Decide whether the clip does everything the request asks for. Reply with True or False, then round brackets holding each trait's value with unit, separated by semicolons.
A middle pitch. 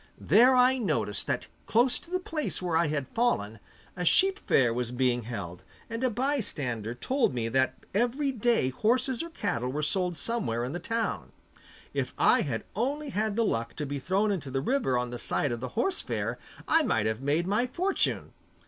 True (180 Hz)